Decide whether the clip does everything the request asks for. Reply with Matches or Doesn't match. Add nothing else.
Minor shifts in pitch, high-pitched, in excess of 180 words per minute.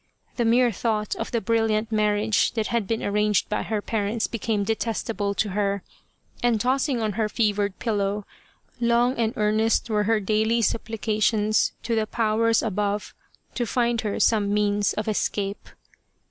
Doesn't match